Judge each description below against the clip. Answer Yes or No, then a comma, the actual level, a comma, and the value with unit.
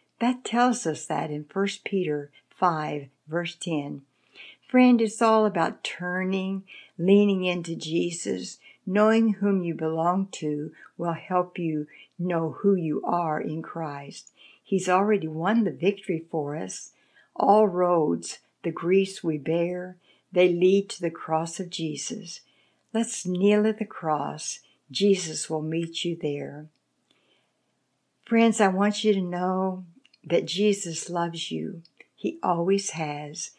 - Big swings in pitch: No, average, 3.8 semitones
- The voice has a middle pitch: Yes, medium, 180 Hz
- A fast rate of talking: No, slow, 135 wpm